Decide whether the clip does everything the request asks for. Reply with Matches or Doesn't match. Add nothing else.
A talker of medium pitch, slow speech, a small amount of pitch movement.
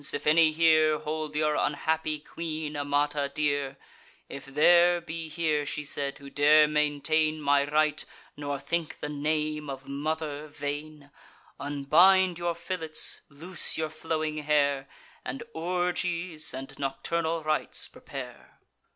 Matches